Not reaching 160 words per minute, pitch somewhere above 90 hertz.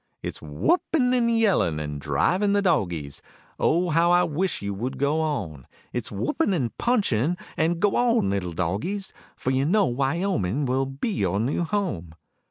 No: average, 165 wpm; medium, 140 Hz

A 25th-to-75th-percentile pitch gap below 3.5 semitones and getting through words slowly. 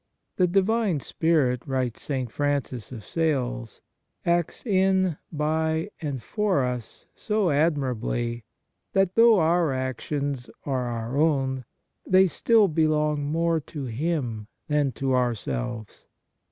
No: average, 5.0 semitones; slow, 125 wpm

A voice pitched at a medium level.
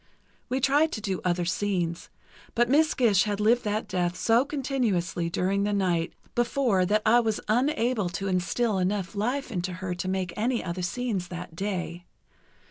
No: high, 200 Hz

